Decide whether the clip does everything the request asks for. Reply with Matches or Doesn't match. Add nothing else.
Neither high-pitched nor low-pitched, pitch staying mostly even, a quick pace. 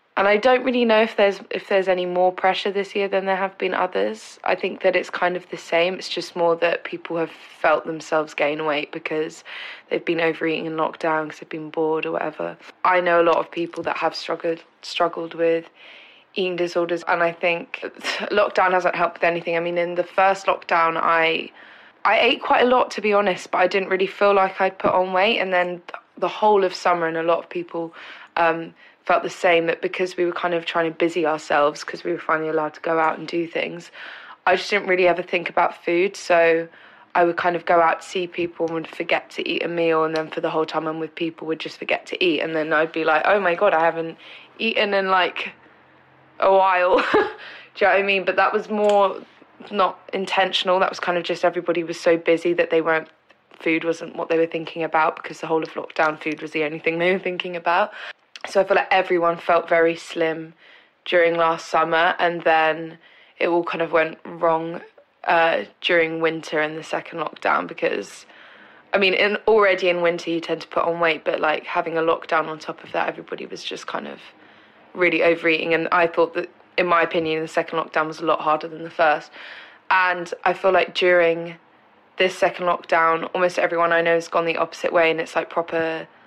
Matches